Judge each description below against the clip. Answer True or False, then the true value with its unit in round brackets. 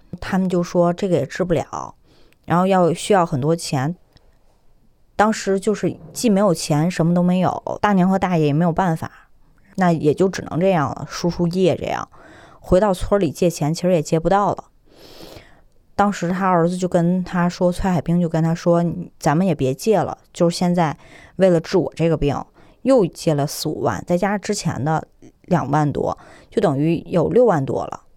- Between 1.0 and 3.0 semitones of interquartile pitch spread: True (2.4 semitones)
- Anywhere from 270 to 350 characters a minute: False (260 characters per minute)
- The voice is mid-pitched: True (175 Hz)